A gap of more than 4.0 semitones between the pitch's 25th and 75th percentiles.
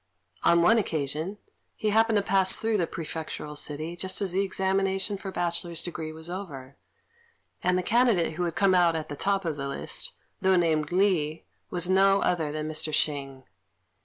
No: average, 3.7 semitones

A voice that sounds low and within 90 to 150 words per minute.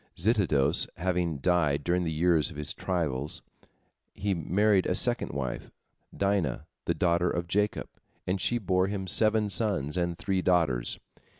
Yes: very low, 90 Hz; average, 145 wpm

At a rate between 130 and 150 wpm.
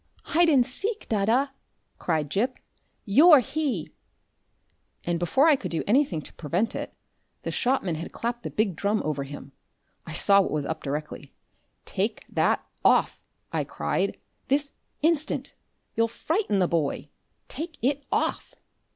Yes: average, 145 wpm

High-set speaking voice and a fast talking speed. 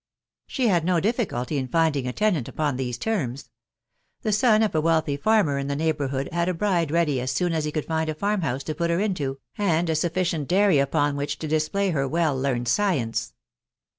No: medium, 160 Hz; fast, 210 wpm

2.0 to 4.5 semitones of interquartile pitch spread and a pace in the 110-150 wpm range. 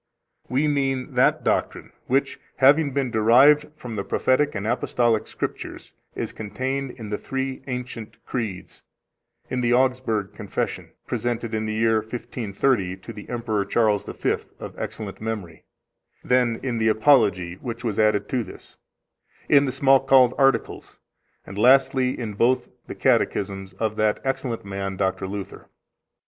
Yes: average, 3.7 semitones; average, 145 wpm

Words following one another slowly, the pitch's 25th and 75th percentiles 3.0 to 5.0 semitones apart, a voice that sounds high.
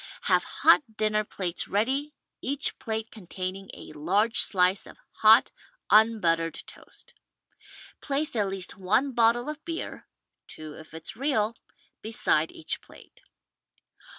Yes: slow, 130 wpm; average, 4.7 semitones; high, 215 Hz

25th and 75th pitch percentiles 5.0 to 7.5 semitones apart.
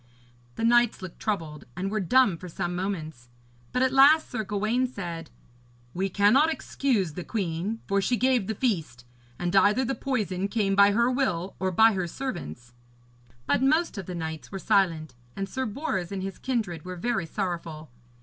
Yes: wide, 5.6 semitones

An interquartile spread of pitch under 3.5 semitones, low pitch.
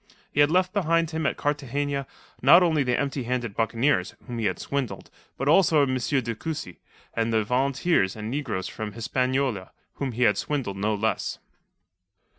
No: average, 4.4 semitones; low, 130 Hz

